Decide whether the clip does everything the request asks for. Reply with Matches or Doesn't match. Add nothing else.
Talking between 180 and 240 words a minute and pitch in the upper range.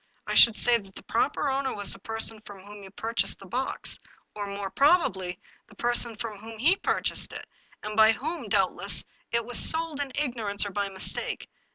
Matches